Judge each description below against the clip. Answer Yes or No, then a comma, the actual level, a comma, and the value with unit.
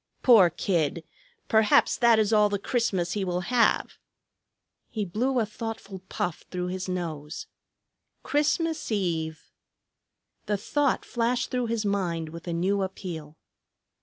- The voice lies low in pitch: No, high, 200 Hz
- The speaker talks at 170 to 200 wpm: No, slow, 135 wpm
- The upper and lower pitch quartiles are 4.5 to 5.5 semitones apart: Yes, average, 4.8 semitones